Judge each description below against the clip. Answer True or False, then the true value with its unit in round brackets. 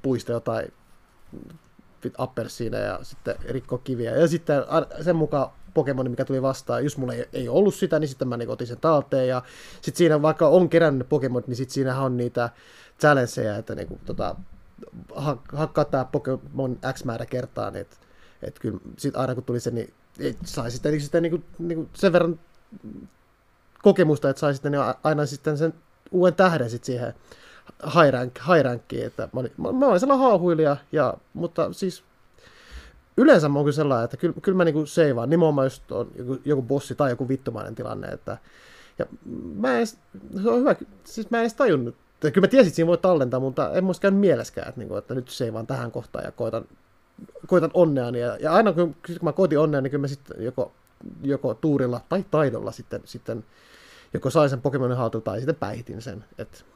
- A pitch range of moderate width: True (5.0 semitones)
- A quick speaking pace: True (185 wpm)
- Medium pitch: True (145 Hz)